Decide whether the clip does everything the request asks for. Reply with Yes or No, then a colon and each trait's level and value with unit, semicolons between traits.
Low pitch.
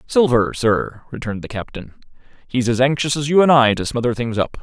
Yes: low, 125 Hz